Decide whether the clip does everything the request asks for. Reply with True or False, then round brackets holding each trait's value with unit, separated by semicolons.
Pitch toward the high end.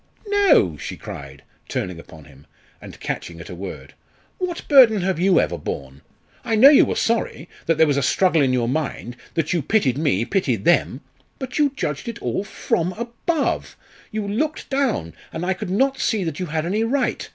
False (180 Hz)